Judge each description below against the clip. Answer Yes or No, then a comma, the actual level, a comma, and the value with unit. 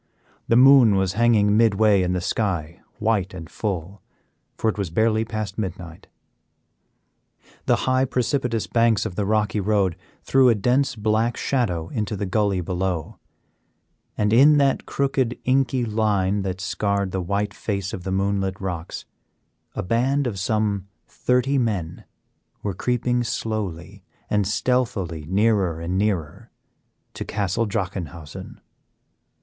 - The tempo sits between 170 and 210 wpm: No, slow, 135 wpm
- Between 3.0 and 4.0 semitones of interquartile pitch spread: Yes, average, 3.6 semitones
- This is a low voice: Yes, low, 105 Hz